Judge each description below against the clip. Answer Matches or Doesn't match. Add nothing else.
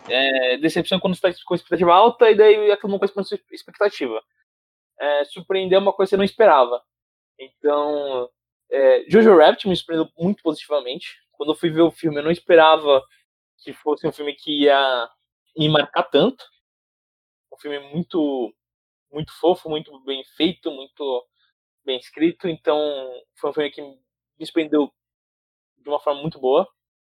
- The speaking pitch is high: Doesn't match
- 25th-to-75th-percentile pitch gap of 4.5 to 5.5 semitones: Matches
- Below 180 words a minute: Matches